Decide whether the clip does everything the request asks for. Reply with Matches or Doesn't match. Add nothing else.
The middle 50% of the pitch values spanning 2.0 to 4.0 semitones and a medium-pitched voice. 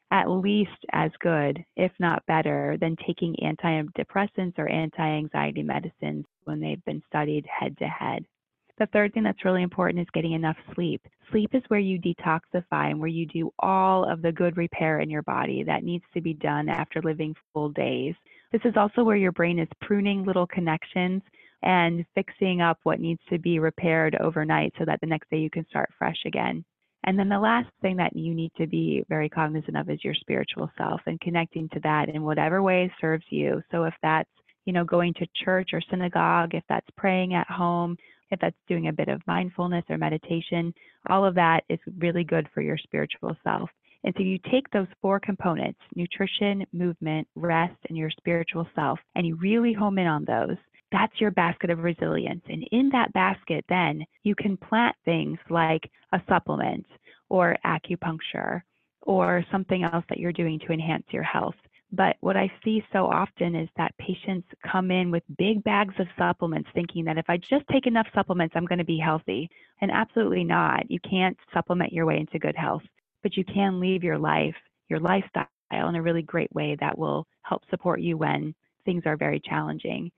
Matches